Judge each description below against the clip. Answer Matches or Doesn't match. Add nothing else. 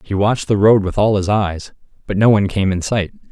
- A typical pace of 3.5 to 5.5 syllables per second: Doesn't match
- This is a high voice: Doesn't match